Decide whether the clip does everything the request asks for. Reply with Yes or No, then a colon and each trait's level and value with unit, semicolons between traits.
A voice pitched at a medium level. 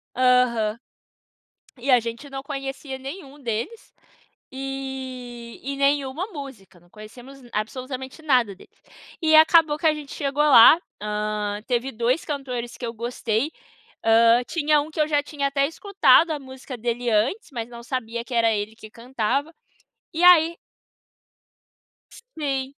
No: very high, 260 Hz